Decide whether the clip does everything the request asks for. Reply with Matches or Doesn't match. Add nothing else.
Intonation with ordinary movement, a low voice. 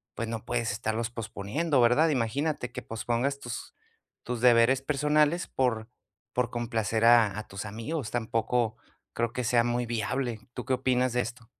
Doesn't match